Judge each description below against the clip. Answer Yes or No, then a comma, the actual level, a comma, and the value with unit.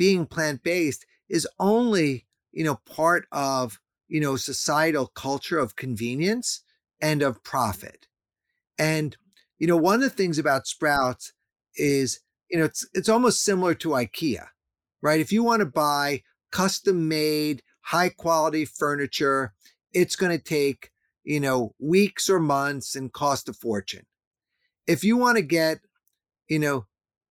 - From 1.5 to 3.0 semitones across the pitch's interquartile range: No, average, 4.9 semitones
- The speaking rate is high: No, average, 145 wpm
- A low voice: No, medium, 155 Hz